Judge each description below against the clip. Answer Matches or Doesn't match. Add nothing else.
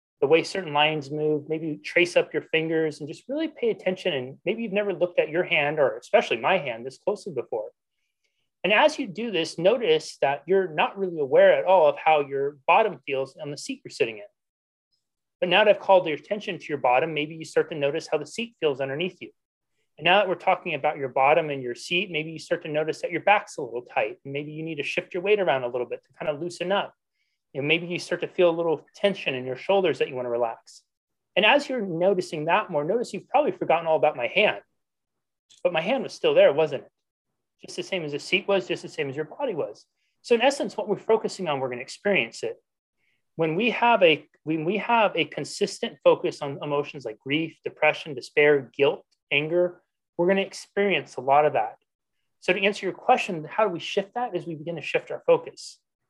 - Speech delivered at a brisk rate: Matches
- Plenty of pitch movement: Matches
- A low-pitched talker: Doesn't match